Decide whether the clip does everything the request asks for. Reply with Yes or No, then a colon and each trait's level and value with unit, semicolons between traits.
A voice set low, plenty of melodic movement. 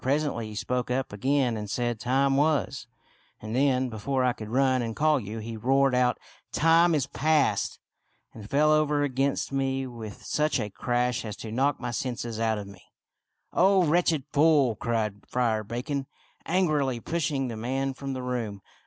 No: low, 130 Hz; average, 3.6 semitones